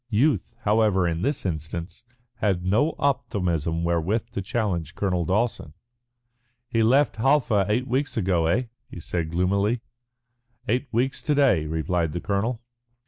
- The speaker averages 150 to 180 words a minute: No, average, 140 wpm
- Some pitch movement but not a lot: No, wide, 5.8 semitones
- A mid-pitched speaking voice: No, low, 100 Hz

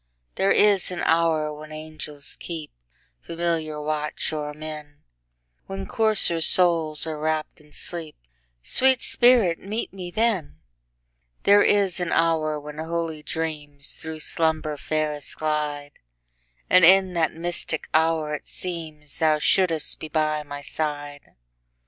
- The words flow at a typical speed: No, slow, 110 wpm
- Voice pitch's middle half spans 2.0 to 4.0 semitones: Yes, narrow, 2.4 semitones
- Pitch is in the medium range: Yes, medium, 155 Hz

